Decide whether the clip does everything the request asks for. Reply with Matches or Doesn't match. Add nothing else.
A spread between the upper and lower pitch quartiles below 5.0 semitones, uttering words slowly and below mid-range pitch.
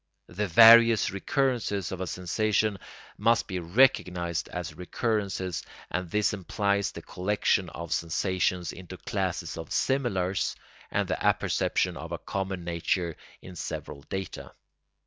Matches